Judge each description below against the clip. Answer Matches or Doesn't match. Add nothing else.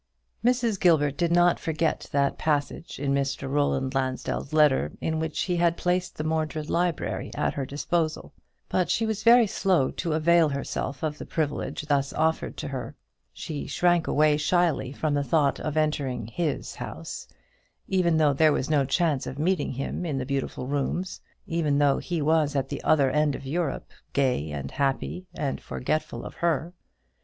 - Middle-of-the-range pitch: Matches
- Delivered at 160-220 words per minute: Matches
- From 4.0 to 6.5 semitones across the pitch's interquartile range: Doesn't match